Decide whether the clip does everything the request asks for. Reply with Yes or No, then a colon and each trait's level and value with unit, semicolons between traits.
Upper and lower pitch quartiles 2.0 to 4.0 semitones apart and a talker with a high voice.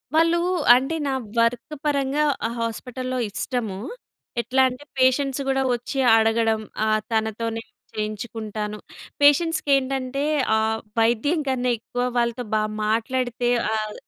Yes: average, 3.3 semitones; high, 245 Hz